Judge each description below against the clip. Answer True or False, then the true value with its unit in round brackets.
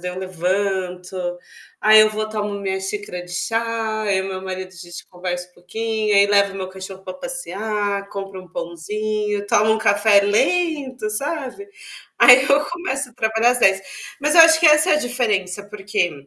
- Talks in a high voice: True (205 Hz)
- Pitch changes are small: False (3.3 semitones)